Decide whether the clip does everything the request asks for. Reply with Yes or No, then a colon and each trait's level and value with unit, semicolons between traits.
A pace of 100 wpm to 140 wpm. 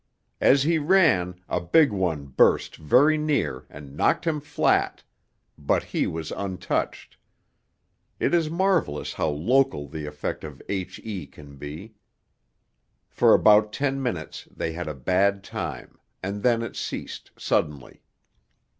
Yes: slow, 135 wpm